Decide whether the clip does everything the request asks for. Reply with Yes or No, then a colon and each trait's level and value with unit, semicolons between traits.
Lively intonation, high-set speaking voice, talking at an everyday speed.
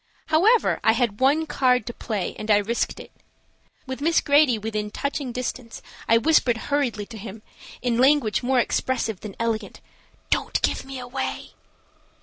No: average, 3.9 semitones; high, 245 Hz; average, 155 wpm